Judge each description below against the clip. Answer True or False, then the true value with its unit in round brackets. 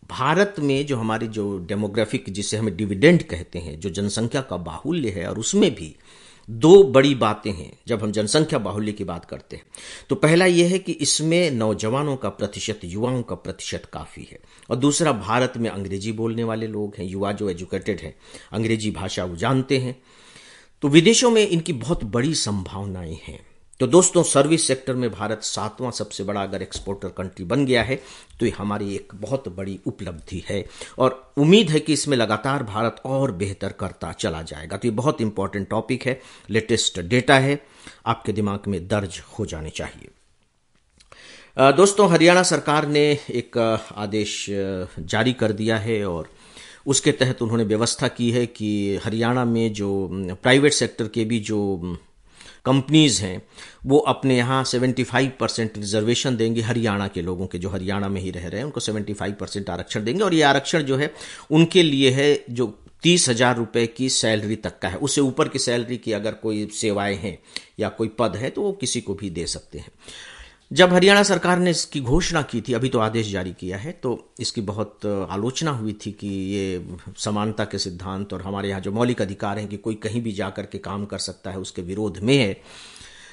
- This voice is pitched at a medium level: False (110 Hz)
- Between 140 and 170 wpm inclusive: False (185 wpm)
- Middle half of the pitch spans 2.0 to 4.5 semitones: False (4.9 semitones)